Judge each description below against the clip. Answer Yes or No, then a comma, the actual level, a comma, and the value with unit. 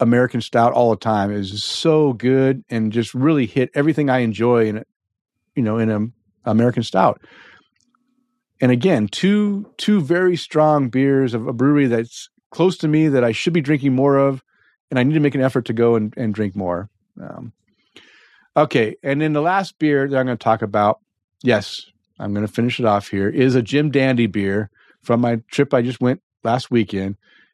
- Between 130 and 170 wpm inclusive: No, average, 200 wpm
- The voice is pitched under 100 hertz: No, low, 125 Hz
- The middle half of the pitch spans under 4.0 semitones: No, average, 4.4 semitones